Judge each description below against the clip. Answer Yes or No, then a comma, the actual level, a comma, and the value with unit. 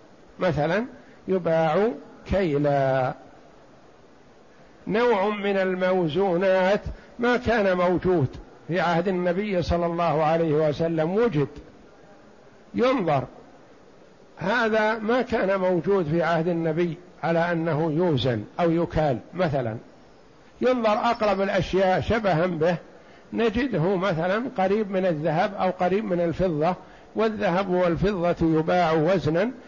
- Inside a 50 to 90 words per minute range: No, average, 100 wpm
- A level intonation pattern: No, average, 3.3 semitones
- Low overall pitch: No, medium, 180 Hz